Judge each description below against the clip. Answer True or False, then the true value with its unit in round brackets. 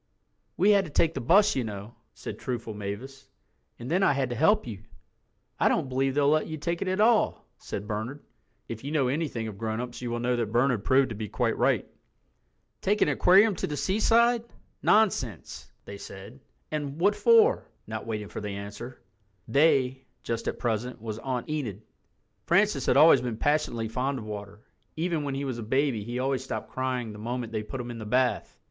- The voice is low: True (130 Hz)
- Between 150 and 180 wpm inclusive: False (200 wpm)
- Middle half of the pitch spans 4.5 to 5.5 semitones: True (5.1 semitones)